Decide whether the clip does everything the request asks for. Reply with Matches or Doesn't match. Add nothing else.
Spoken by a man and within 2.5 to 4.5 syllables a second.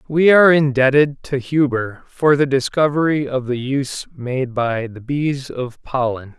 Matches